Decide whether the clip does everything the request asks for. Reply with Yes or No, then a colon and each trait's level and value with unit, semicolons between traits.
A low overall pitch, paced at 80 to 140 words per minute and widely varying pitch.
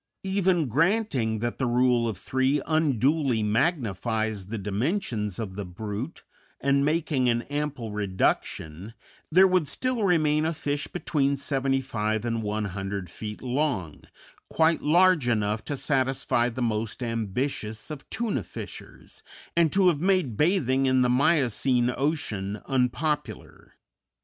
Yes: low, 130 Hz; slow, 135 wpm; wide, 5.7 semitones